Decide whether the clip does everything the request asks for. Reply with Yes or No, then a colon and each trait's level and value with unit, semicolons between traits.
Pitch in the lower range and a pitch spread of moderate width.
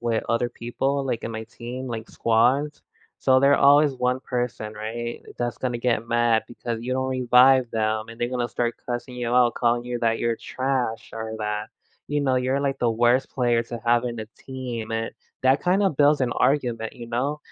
No: low, 120 Hz; narrow, 2.1 semitones